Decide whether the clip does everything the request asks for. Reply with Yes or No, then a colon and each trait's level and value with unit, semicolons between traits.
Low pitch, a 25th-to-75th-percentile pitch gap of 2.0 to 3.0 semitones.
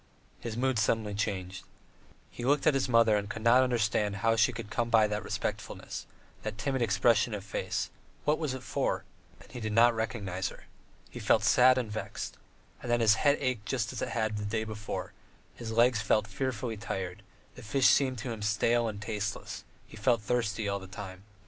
Yes: low, 110 Hz; narrow, 2.5 semitones